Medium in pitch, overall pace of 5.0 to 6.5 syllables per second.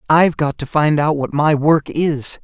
No: medium, 150 Hz; 4.5 syllables/s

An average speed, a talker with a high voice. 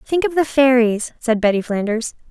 Yes: average, 185 wpm; high, 245 Hz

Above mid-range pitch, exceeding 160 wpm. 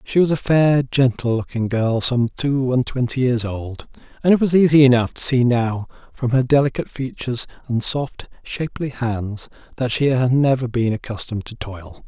No: low, 125 Hz; average, 185 wpm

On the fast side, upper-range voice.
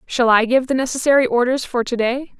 Yes: fast, 225 wpm; very high, 250 Hz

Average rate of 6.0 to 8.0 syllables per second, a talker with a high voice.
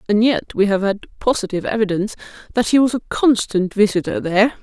Yes: 6.1 syllables/s; high, 215 Hz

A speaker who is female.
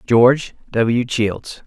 No: male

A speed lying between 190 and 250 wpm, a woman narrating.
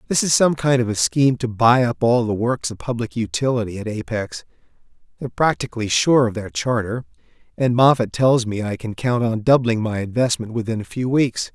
No: fast, 205 wpm; male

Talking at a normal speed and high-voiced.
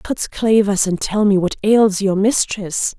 Yes: average, 180 wpm; high, 205 Hz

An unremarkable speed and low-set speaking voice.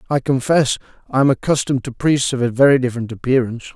Yes: average, 190 wpm; low, 130 Hz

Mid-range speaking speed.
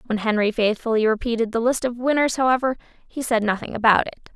Yes: average, 195 wpm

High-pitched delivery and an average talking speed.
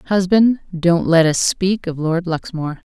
No: medium, 175 Hz; average, 165 wpm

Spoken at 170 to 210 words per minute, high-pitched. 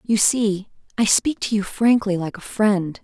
Yes: average, 200 wpm; high, 210 Hz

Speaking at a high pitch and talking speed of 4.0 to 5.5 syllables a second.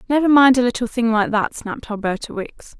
No: high, 235 Hz; 5.8 syllables/s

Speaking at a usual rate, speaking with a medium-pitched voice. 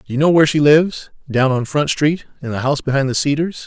No: fast, 245 wpm; medium, 145 Hz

